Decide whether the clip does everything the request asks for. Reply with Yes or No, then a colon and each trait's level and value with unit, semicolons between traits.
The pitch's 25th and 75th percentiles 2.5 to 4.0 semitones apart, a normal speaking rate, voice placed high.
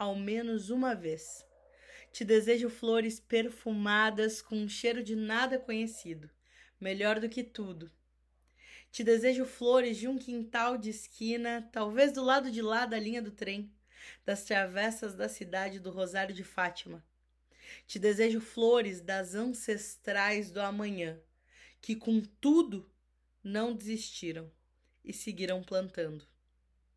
Yes: average, 3.4 semitones; average, 130 wpm; high, 215 Hz